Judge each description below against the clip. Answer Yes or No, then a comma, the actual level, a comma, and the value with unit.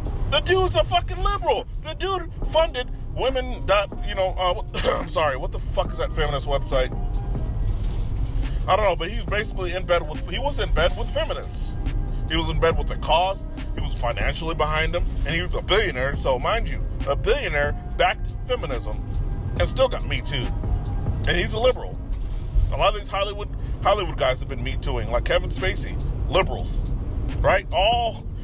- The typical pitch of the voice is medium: Yes, medium, 155 Hz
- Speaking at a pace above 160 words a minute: Yes, average, 185 wpm